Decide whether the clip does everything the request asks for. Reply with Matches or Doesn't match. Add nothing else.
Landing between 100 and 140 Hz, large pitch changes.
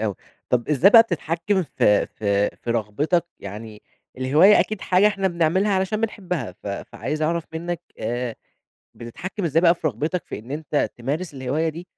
Doesn't match